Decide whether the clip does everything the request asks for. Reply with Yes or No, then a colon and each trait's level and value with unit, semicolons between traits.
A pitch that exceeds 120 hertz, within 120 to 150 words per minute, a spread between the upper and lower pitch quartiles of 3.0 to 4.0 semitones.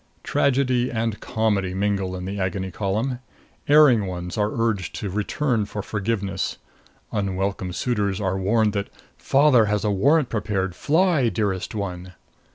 No: low, 105 Hz; slow, 135 wpm; average, 3.4 semitones